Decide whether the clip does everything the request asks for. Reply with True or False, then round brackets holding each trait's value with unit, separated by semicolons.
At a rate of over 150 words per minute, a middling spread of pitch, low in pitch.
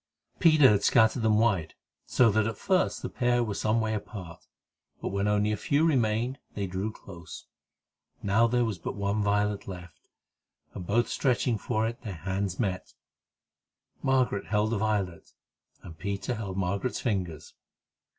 True (160 wpm; 3.0 semitones; 105 Hz)